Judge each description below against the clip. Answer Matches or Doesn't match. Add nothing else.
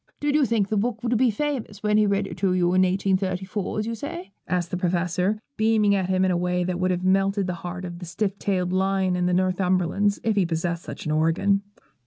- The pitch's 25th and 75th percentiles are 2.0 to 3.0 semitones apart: Matches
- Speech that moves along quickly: Matches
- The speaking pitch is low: Doesn't match